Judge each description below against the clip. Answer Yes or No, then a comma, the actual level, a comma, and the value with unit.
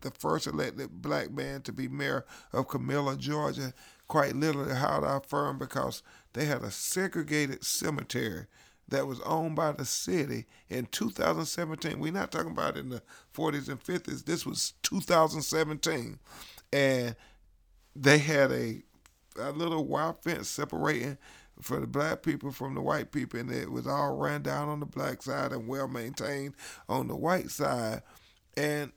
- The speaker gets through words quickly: No, average, 160 wpm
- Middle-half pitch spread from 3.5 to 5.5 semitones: No, average, 2.7 semitones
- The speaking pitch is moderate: Yes, medium, 145 Hz